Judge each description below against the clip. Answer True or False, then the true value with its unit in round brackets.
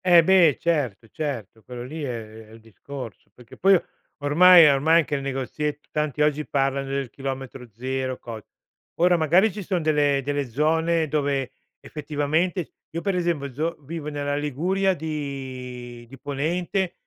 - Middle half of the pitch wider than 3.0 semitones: True (3.7 semitones)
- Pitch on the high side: False (145 Hz)